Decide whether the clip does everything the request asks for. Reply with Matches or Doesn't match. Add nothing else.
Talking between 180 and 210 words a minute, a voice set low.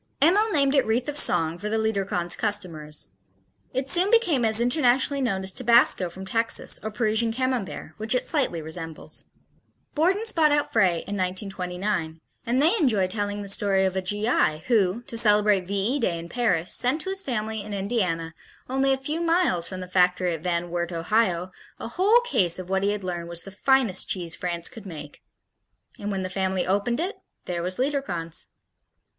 Doesn't match